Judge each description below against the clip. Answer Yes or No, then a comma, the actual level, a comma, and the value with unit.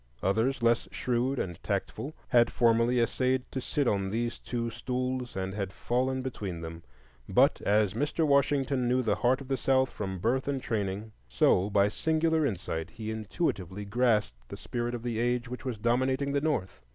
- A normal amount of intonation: Yes, average, 4.1 semitones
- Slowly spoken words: No, average, 175 wpm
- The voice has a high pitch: No, low, 120 Hz